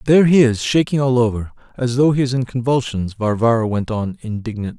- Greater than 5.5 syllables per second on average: Yes, 6.0 syllables/s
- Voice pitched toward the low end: Yes, low, 120 Hz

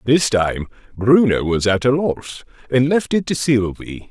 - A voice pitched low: Yes, low, 125 Hz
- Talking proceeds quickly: No, average, 175 wpm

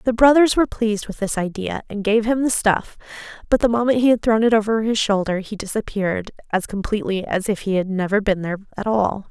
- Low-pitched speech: No, high, 210 Hz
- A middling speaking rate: No, fast, 225 wpm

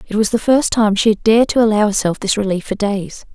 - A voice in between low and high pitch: No, high, 210 Hz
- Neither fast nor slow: No, fast, 270 wpm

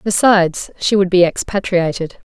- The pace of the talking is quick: No, slow, 130 wpm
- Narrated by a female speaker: Yes, female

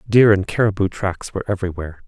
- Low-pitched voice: Yes, low, 100 Hz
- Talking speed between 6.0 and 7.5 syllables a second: Yes, 6.8 syllables/s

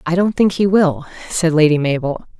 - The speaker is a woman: Yes, female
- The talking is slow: No, average, 200 wpm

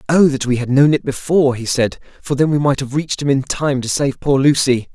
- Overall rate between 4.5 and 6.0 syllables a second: Yes, 5.7 syllables/s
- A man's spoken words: Yes, male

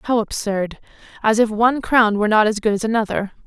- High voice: Yes, high, 220 Hz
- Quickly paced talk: No, average, 190 wpm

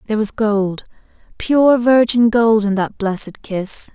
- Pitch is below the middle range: No, high, 220 Hz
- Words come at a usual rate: Yes, average, 150 wpm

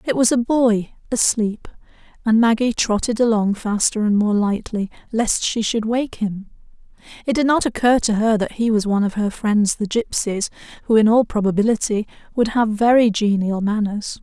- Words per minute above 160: Yes, average, 175 wpm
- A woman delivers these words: Yes, female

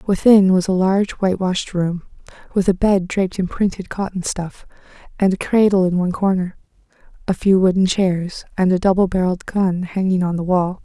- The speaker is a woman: Yes, female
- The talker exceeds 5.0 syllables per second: Yes, 5.5 syllables/s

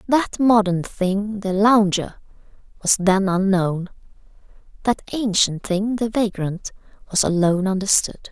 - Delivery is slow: Yes, slow, 115 wpm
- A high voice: Yes, high, 200 Hz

